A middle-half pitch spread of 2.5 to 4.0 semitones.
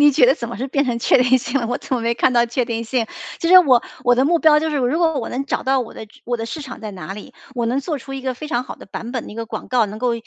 Yes: average, 2.9 semitones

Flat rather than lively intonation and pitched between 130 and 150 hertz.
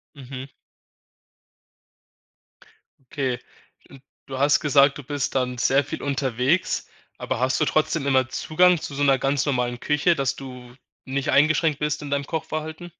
Yes: narrow, 2.3 semitones; medium, 140 Hz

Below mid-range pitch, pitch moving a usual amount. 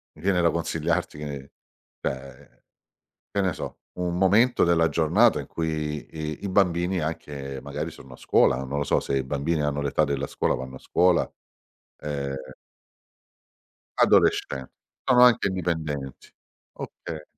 Yes: very low, 75 Hz; average, 3.8 semitones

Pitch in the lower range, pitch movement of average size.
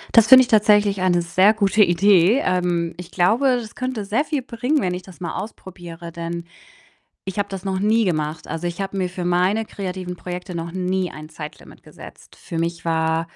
No: medium, 185 Hz; average, 3.3 semitones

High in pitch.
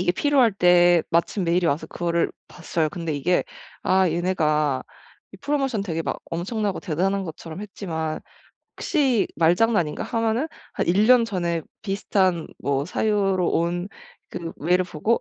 No: medium, 180 Hz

